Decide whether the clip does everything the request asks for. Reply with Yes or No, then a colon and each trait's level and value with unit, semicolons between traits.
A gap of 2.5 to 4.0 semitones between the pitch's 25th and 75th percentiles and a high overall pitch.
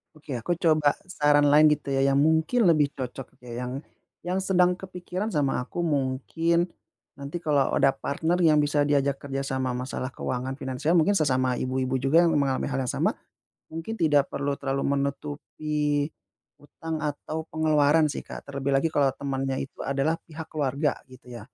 No: average, 2.9 semitones; medium, 145 Hz